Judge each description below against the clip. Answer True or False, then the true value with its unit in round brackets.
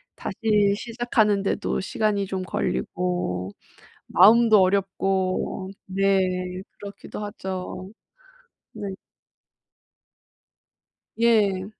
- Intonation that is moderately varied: False (2.1 semitones)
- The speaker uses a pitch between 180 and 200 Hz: True (195 Hz)